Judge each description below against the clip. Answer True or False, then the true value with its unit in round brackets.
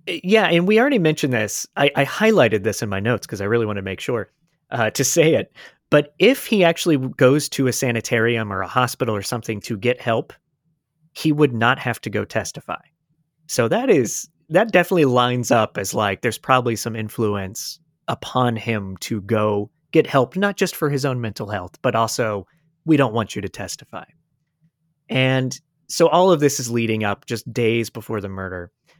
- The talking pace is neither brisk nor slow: True (195 wpm)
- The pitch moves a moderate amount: False (6.0 semitones)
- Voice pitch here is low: True (125 Hz)